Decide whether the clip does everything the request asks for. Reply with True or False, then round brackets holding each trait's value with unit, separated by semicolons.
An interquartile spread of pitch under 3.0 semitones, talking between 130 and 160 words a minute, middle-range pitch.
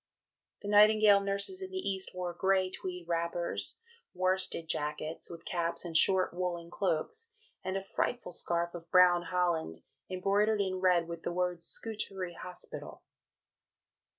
True (2.4 semitones; 145 wpm; 180 Hz)